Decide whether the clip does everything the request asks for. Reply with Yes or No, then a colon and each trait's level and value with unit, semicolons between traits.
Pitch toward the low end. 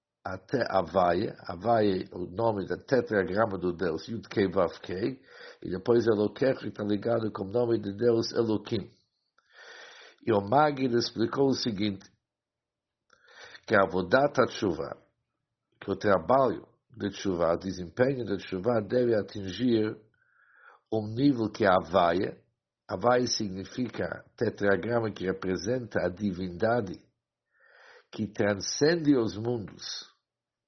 Yes: low, 110 Hz